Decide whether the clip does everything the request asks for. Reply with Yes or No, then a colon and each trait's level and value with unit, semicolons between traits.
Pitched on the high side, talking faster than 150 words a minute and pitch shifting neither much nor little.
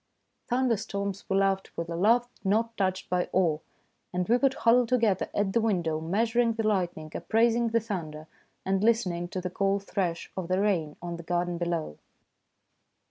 Yes: high, 195 Hz; average, 175 wpm; average, 4.4 semitones